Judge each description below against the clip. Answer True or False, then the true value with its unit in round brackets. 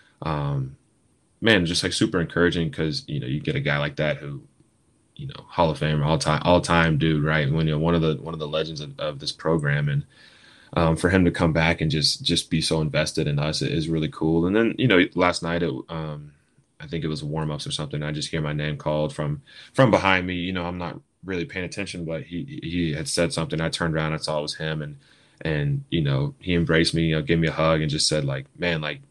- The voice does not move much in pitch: True (2.1 semitones)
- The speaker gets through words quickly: True (260 wpm)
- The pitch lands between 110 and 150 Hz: False (80 Hz)